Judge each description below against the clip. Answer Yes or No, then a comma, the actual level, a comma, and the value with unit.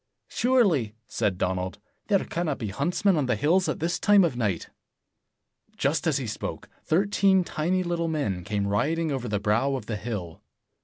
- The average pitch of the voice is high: No, medium, 140 Hz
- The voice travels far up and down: Yes, wide, 8.8 semitones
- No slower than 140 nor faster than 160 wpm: No, average, 175 wpm